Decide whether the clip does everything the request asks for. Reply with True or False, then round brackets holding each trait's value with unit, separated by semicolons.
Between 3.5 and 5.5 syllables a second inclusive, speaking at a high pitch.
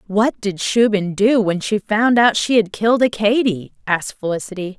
True (4.9 syllables/s; 210 Hz)